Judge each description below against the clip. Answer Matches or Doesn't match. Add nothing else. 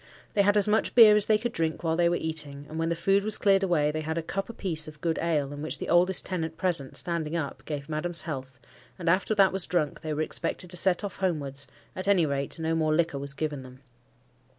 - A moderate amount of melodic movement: Matches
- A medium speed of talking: Doesn't match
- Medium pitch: Matches